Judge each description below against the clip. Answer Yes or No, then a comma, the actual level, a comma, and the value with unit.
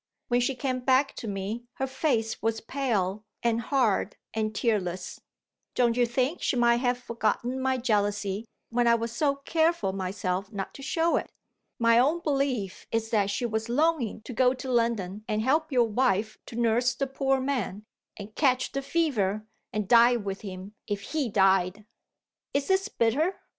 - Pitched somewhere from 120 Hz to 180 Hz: No, high, 235 Hz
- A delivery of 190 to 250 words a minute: No, average, 175 wpm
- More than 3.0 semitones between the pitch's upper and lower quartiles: Yes, average, 4.0 semitones